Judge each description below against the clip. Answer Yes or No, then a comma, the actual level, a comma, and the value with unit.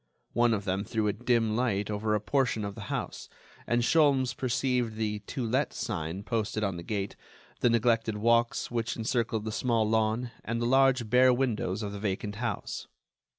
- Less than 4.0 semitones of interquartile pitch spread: Yes, average, 2.7 semitones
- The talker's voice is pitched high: No, low, 115 Hz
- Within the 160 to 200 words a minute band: Yes, average, 185 wpm